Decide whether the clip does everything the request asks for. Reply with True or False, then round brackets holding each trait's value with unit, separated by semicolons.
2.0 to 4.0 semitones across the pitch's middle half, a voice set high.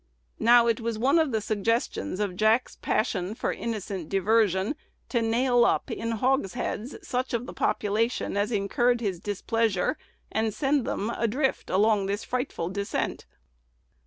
True (3.0 semitones; 225 Hz)